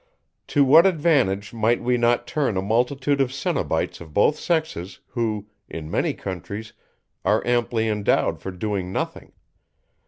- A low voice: Yes, low, 115 Hz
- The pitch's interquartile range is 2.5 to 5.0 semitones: No, wide, 5.4 semitones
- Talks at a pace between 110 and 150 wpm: Yes, average, 145 wpm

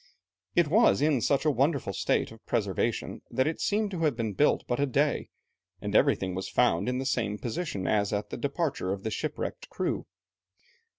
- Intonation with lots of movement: Yes, wide, 6.6 semitones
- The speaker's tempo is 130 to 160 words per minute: No, average, 190 wpm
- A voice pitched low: Yes, low, 130 Hz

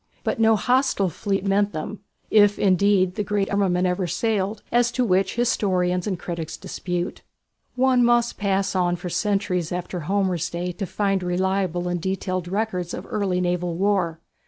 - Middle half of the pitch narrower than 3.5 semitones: Yes, narrow, 2.4 semitones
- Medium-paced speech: Yes, average, 160 wpm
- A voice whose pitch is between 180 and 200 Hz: Yes, high, 190 Hz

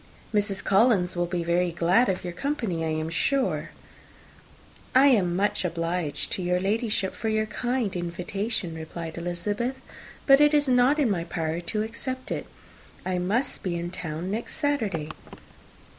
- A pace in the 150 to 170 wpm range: Yes, average, 160 wpm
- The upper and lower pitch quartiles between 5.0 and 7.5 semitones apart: Yes, average, 5.3 semitones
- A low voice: No, high, 190 Hz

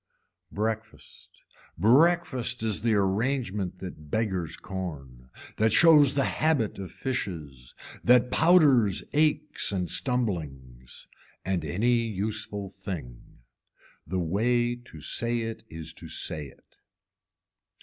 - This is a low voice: Yes, low, 105 Hz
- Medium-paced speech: No, slow, 110 wpm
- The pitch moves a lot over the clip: Yes, wide, 5.7 semitones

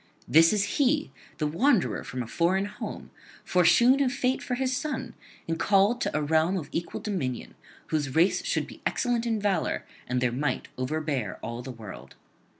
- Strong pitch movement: Yes, wide, 8.5 semitones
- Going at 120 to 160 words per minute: No, average, 175 wpm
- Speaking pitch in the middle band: Yes, medium, 175 Hz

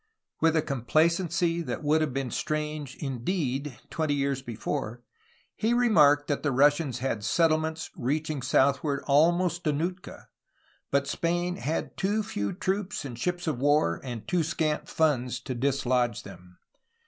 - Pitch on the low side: No, medium, 150 Hz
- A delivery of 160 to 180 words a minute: No, average, 150 wpm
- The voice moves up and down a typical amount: Yes, average, 4.0 semitones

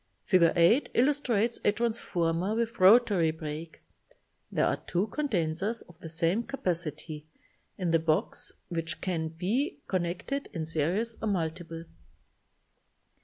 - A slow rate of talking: Yes, slow, 120 wpm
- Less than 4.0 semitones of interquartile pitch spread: No, wide, 5.5 semitones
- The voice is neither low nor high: Yes, medium, 175 Hz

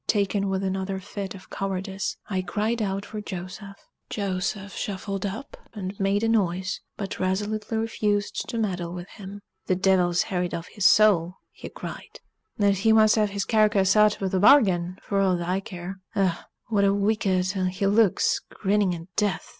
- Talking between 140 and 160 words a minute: No, average, 170 wpm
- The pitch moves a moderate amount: No, narrow, 2.0 semitones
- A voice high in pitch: Yes, high, 195 Hz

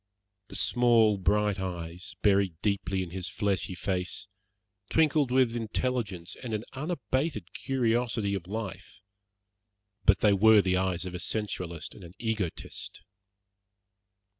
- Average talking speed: No, slow, 125 wpm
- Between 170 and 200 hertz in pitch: No, low, 100 Hz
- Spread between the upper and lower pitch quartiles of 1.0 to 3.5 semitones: No, average, 4.0 semitones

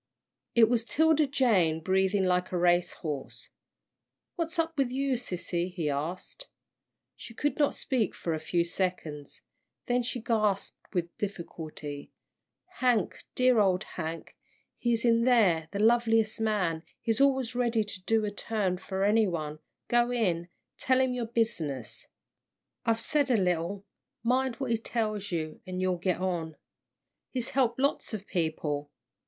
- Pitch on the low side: No, high, 210 Hz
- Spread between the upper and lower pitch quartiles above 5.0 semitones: Yes, wide, 5.6 semitones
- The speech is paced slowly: No, average, 150 wpm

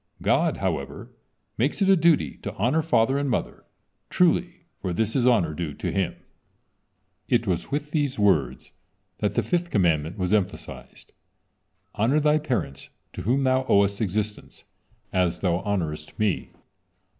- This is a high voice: No, low, 110 Hz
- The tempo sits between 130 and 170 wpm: Yes, average, 145 wpm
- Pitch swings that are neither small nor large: No, wide, 7.6 semitones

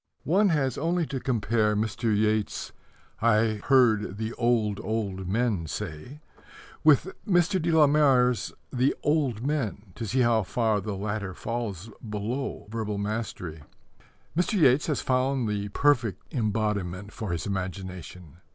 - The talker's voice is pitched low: Yes, low, 110 Hz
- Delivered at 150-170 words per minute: No, slow, 135 wpm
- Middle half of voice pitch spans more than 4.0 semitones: Yes, average, 4.5 semitones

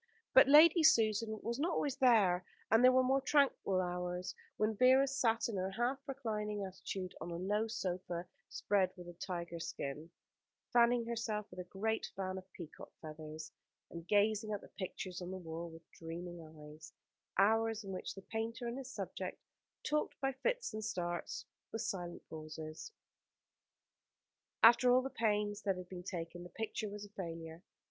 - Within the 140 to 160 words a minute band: No, average, 170 wpm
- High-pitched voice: Yes, high, 205 Hz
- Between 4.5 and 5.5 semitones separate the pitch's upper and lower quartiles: Yes, average, 4.8 semitones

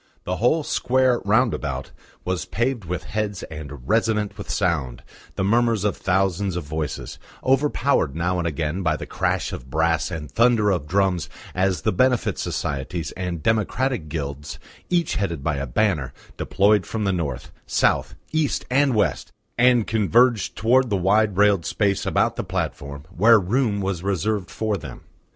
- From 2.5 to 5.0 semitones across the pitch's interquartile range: No, wide, 5.5 semitones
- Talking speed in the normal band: Yes, average, 160 wpm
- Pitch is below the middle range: Yes, very low, 95 Hz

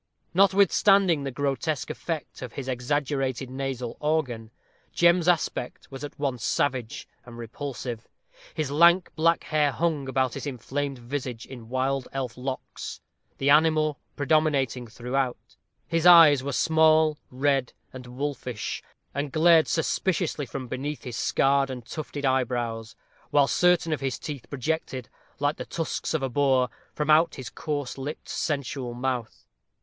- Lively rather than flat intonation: No, average, 3.4 semitones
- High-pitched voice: No, medium, 140 Hz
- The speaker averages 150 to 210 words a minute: No, average, 140 wpm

